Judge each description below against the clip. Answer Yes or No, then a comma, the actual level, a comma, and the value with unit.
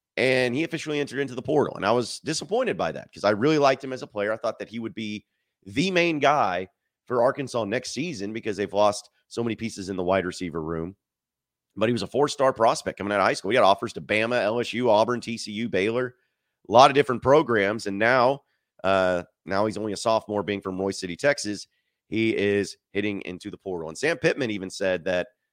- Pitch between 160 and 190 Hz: No, low, 105 Hz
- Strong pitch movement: No, average, 4.1 semitones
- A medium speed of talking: No, fast, 225 wpm